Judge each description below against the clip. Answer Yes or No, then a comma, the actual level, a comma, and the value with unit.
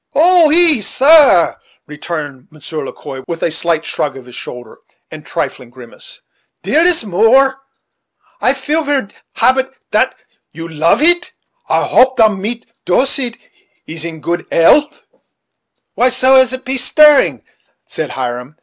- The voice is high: Yes, high, 225 Hz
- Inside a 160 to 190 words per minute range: No, average, 150 wpm